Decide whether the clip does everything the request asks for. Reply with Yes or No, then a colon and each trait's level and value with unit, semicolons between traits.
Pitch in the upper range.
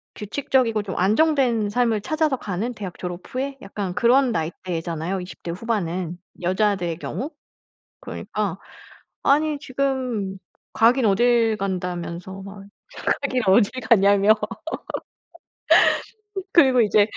Yes: high, 210 Hz